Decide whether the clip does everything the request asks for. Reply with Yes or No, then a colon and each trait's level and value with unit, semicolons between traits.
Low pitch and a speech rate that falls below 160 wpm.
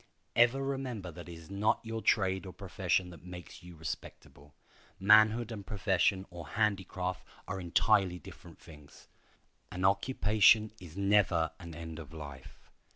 Yes: very low, 95 Hz; average, 145 wpm